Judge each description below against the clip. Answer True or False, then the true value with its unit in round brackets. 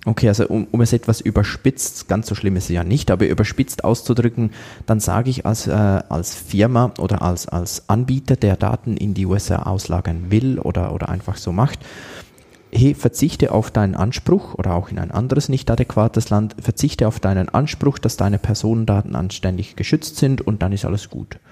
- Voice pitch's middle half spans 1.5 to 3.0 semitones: False (3.7 semitones)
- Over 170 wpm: True (190 wpm)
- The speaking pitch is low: True (110 Hz)